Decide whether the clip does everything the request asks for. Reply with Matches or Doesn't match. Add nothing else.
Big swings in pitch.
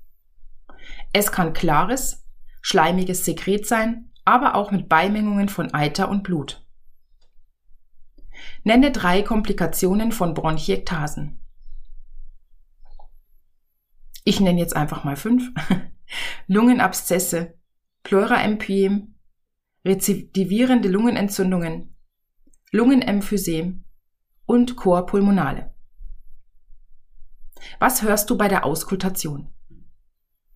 Matches